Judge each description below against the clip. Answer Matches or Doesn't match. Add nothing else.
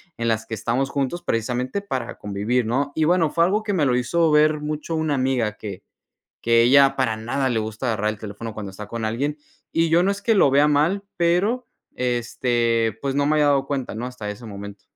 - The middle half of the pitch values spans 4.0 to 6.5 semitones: Matches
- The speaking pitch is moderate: Doesn't match